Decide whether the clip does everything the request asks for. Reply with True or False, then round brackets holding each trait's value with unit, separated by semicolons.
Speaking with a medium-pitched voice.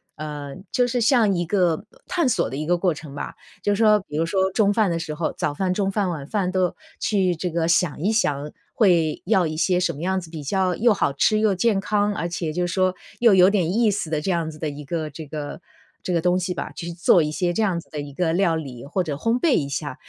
True (175 Hz)